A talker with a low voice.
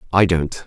Yes: very low, 85 Hz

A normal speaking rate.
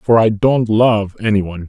No: fast, 215 wpm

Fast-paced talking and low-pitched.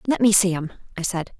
No: fast, 260 wpm; high, 190 Hz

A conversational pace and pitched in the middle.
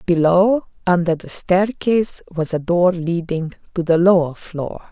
Yes: average, 145 wpm; medium, 175 Hz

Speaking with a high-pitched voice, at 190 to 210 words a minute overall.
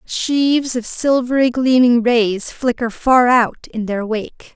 No: high, 245 Hz; average, 145 wpm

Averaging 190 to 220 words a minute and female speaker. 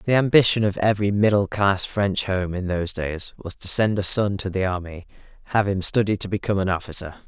No: fast, 205 wpm; male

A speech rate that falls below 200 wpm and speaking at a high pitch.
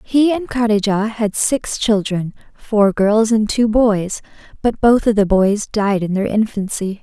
Yes: average, 170 wpm; high, 215 Hz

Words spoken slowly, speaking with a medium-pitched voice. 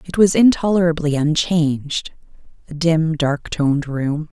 Yes: slow, 125 wpm; medium, 160 Hz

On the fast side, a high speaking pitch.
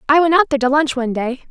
Yes: fast, 320 wpm; very high, 280 Hz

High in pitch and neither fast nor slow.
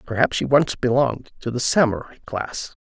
No: low, 125 Hz; average, 170 wpm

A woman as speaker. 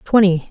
Yes: female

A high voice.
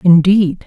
No: medium, 180 Hz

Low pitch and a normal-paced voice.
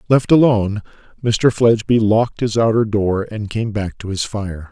Yes: low, 110 Hz; average, 180 wpm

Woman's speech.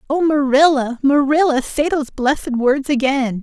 Yes: female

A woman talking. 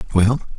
No: male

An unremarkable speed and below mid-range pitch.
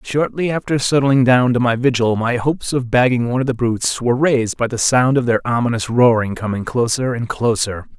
No: fast, 210 wpm; low, 120 Hz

